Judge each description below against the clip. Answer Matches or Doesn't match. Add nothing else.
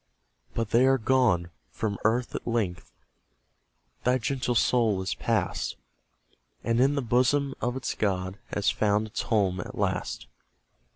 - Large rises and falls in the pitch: Doesn't match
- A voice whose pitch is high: Doesn't match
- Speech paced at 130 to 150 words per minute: Matches